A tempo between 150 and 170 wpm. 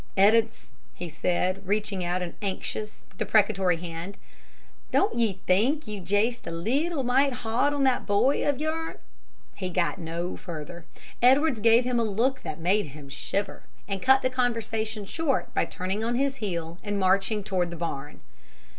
Yes: average, 165 wpm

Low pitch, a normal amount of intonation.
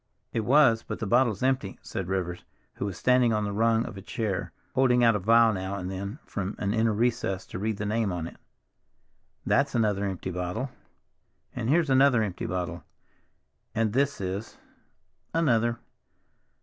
Yes: low, 110 Hz; average, 4.0 semitones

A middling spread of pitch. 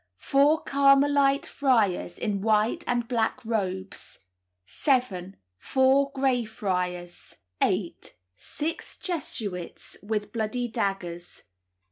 No: wide, 5.9 semitones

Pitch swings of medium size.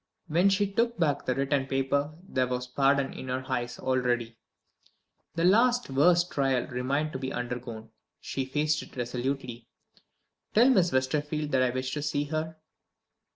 Yes: average, 3.3 semitones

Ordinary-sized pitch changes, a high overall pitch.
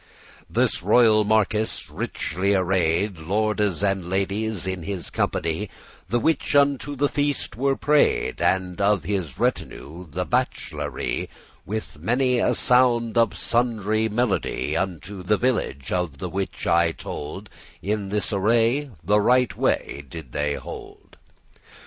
No: average, 4.3 semitones; low, 100 Hz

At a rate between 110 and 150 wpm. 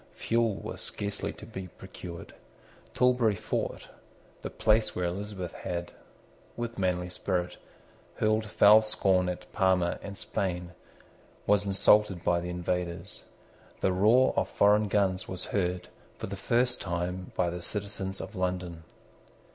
Yes: slow, 135 wpm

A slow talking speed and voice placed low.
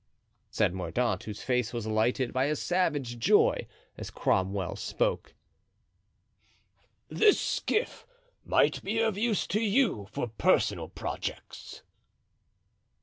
Yes: slow, 110 wpm; low, 125 Hz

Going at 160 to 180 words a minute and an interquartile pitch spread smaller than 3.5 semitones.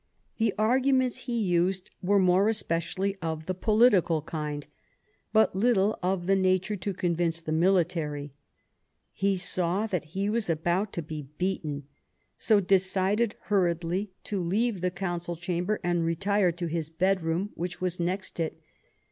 No: average, 150 wpm; average, 3.0 semitones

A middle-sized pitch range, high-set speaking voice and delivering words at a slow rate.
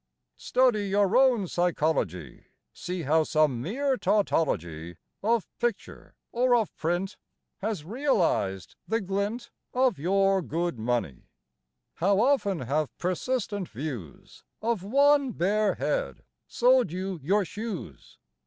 No: wide, 7.0 semitones; high, 195 Hz; slow, 115 wpm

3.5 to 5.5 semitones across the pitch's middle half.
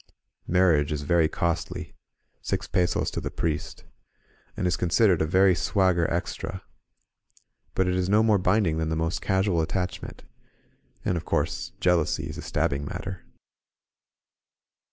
No: narrow, 2.6 semitones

